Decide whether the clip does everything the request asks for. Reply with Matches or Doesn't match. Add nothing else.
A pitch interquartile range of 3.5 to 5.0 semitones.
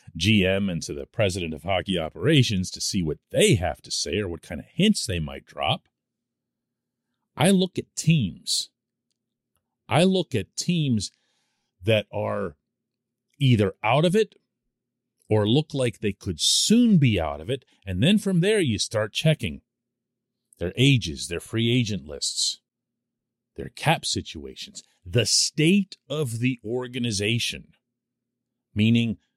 Matches